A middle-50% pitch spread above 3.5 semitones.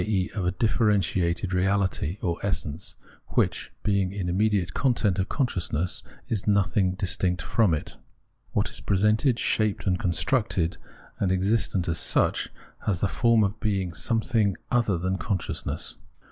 No: average, 3.0 semitones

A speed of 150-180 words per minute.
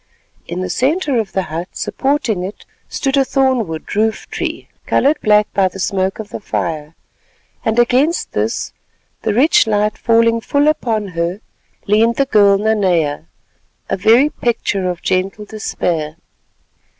No: average, 140 wpm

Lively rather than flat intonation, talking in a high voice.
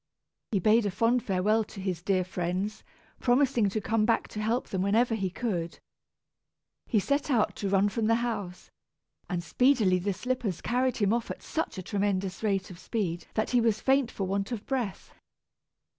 No: average, 3.7 semitones; high, 210 Hz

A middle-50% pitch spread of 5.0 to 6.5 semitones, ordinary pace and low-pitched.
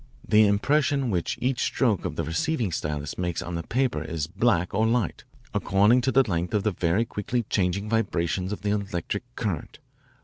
Yes: wide, 5.4 semitones; average, 180 wpm; low, 105 Hz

